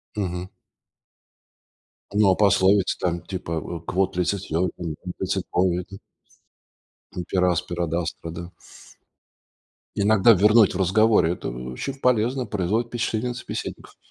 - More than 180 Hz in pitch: No, very low, 95 Hz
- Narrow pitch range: No, average, 3.5 semitones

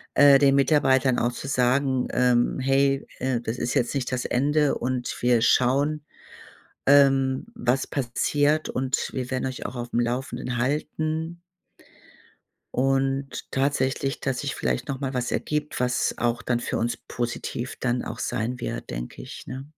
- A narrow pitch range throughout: Yes, narrow, 2.1 semitones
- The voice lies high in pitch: No, low, 130 Hz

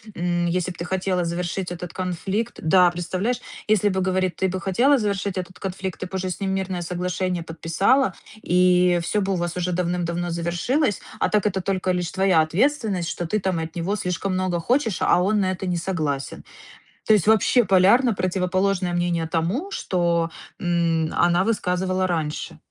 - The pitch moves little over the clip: Yes, narrow, 1.9 semitones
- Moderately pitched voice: Yes, medium, 180 Hz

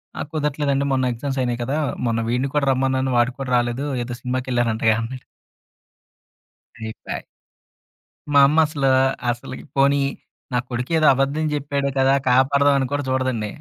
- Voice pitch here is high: No, low, 130 Hz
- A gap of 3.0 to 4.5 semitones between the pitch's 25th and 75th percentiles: No, narrow, 2.4 semitones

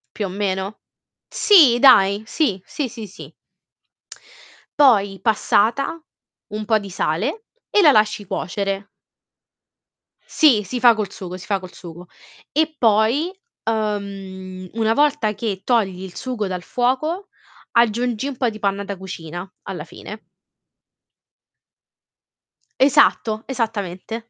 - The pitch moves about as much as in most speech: Yes, average, 4.3 semitones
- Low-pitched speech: No, high, 215 Hz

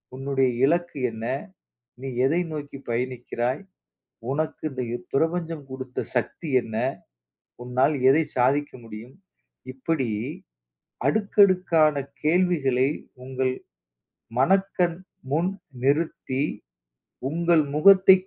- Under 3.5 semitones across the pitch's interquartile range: No, average, 4.5 semitones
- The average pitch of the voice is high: No, medium, 145 Hz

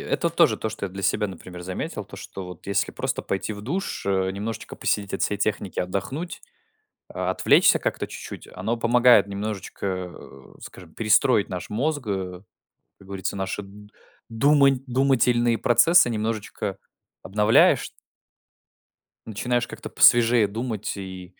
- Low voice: Yes, low, 105 Hz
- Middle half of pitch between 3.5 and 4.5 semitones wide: Yes, average, 3.8 semitones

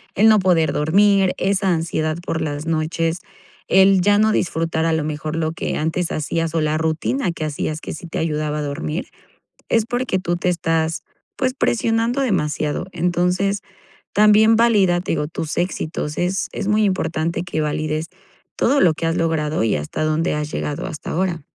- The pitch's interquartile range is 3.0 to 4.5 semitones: Yes, average, 3.7 semitones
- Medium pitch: Yes, medium, 165 Hz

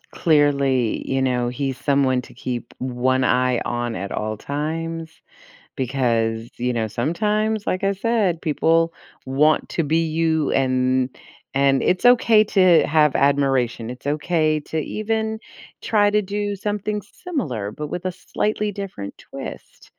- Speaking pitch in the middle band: Yes, medium, 150 Hz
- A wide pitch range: Yes, wide, 6.7 semitones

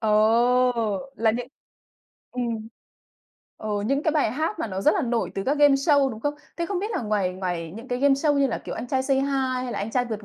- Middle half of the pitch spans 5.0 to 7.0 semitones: No, average, 4.1 semitones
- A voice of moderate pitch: No, very high, 250 Hz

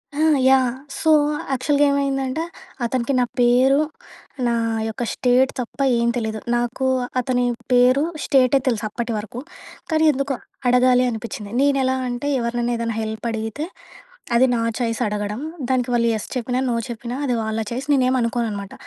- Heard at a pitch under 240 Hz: No, high, 245 Hz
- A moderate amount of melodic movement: No, narrow, 2.1 semitones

